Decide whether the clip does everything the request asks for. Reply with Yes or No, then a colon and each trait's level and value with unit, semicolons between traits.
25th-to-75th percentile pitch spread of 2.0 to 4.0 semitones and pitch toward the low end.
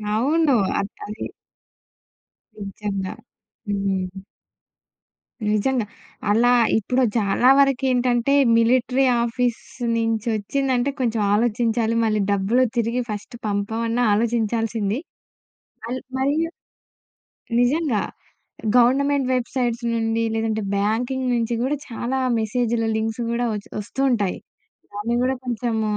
No: narrow, 2.6 semitones; high, 235 Hz